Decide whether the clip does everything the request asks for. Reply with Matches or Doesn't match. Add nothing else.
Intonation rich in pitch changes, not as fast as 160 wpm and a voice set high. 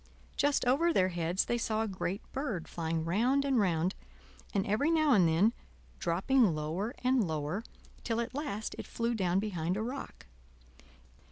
Doesn't match